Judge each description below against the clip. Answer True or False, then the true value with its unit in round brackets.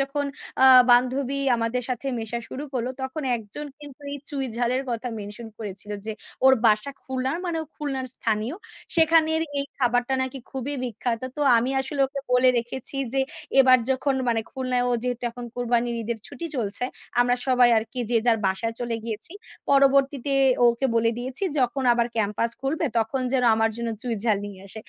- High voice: True (250 Hz)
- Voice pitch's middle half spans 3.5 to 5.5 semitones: False (2.8 semitones)